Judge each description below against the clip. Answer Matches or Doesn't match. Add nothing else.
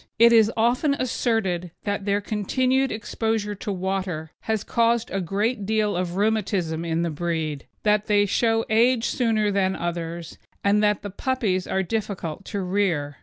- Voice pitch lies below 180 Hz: Doesn't match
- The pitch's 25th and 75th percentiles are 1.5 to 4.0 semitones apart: Matches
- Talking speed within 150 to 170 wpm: Matches